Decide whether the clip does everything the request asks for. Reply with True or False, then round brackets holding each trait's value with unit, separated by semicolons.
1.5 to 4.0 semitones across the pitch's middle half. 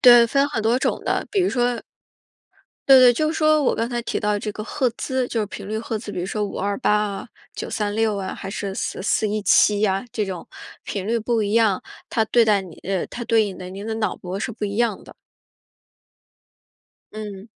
True (2.9 semitones)